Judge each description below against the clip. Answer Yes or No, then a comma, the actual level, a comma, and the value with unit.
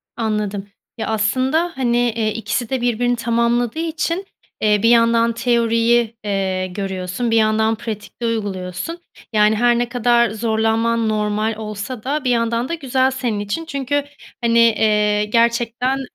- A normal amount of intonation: No, narrow, 2.3 semitones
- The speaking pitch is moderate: No, high, 230 Hz